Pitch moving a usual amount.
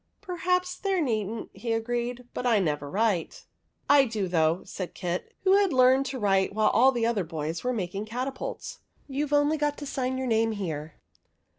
No: wide, 5.9 semitones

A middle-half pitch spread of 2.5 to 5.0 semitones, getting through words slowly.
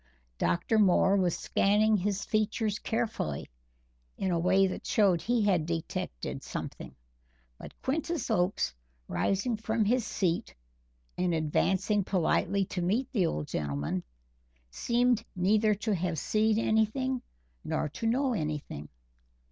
Yes: average, 4.1 semitones; slow, 125 wpm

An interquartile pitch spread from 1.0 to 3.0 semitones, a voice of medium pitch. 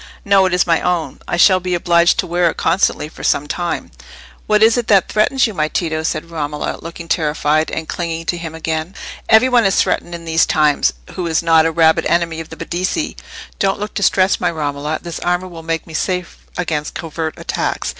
Yes: narrow, 2.5 semitones; medium, 170 Hz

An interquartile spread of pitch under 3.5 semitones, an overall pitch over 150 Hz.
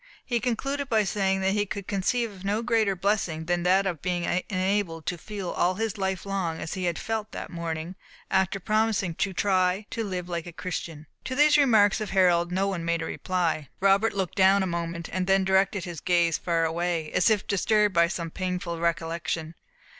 Yes: average, 3.0 semitones; medium, 185 Hz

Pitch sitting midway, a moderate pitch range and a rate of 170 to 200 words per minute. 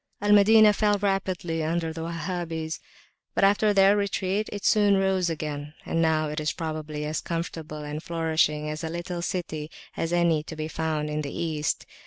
Yes: medium, 165 Hz; average, 3.7 semitones; average, 175 wpm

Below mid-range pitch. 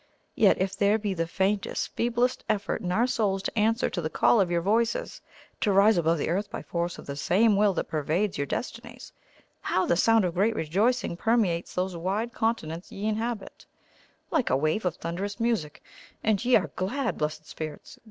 No: high, 200 Hz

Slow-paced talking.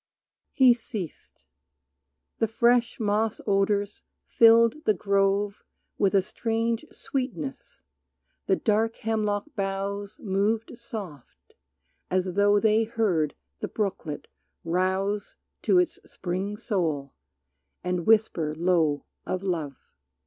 Yes: slow, 105 wpm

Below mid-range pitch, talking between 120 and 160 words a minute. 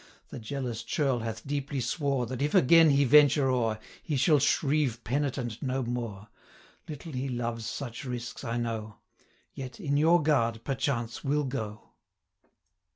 Yes: low, 130 Hz; average, 155 wpm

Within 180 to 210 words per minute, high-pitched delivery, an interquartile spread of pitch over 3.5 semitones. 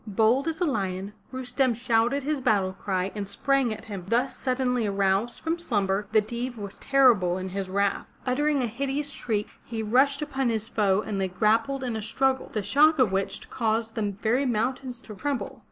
Yes: average, 190 wpm; high, 230 Hz; average, 4.7 semitones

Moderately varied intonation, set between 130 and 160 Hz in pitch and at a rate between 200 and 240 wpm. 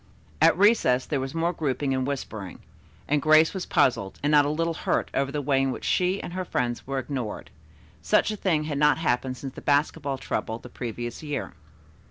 Yes: average, 3.5 semitones; medium, 140 Hz; fast, 205 wpm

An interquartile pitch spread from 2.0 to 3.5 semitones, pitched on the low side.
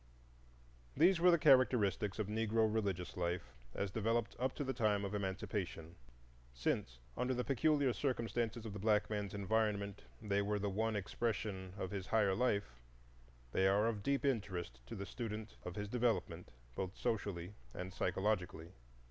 Yes: average, 3.2 semitones; low, 105 Hz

